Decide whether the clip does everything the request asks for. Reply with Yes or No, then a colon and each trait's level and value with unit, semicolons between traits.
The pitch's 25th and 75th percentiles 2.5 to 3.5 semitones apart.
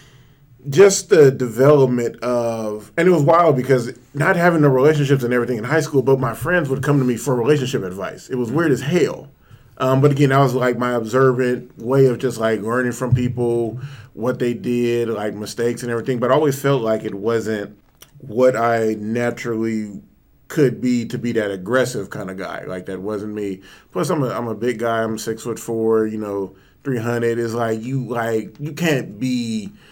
Yes: average, 3.0 semitones